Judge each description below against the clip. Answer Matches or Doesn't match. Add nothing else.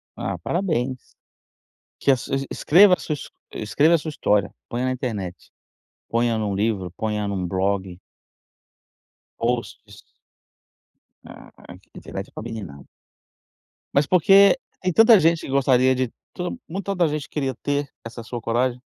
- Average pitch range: Doesn't match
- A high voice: Doesn't match